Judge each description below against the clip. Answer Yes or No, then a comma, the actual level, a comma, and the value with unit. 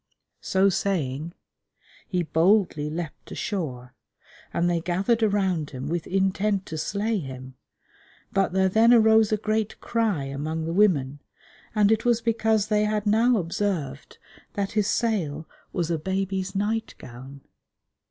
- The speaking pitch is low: No, high, 190 Hz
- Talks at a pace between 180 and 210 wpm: No, average, 140 wpm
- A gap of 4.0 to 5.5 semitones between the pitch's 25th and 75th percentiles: Yes, average, 5.1 semitones